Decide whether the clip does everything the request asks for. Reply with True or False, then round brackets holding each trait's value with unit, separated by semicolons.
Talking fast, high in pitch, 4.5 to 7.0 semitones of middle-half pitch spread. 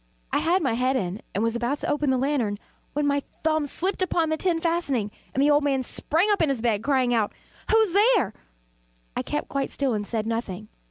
True (215 wpm; 275 Hz; 5.6 semitones)